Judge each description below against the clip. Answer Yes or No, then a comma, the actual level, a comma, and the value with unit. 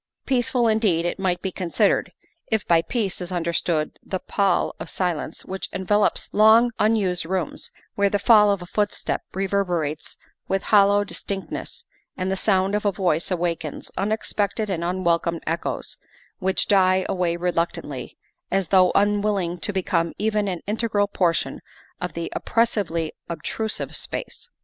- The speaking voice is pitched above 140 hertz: Yes, high, 190 Hz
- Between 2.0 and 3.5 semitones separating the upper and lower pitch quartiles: Yes, average, 3.0 semitones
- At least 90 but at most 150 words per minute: Yes, average, 145 wpm